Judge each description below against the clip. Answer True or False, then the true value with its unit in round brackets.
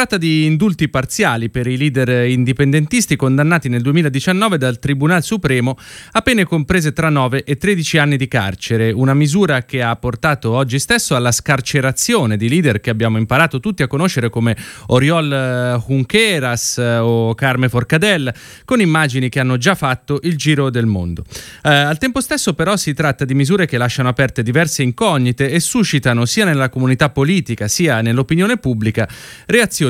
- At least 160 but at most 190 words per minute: True (165 wpm)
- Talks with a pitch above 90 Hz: True (135 Hz)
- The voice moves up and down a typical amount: True (4.7 semitones)